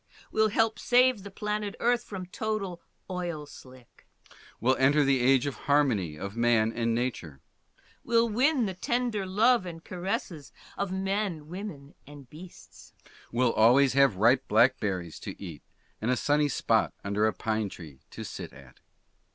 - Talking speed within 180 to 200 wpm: No, average, 155 wpm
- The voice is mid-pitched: Yes, medium, 145 Hz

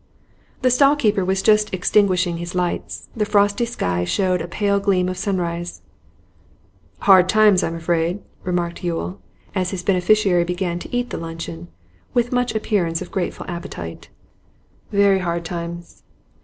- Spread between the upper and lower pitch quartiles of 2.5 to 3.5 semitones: Yes, average, 3.0 semitones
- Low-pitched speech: No, medium, 185 Hz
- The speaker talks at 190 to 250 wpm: No, average, 145 wpm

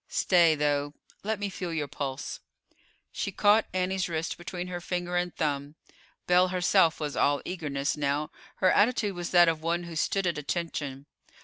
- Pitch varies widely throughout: No, average, 3.5 semitones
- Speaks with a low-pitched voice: No, medium, 170 Hz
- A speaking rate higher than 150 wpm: Yes, average, 170 wpm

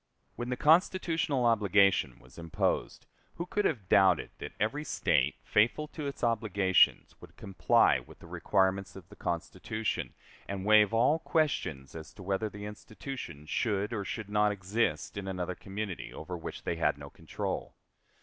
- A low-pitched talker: Yes, low, 105 Hz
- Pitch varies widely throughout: No, average, 4.0 semitones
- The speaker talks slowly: No, average, 160 wpm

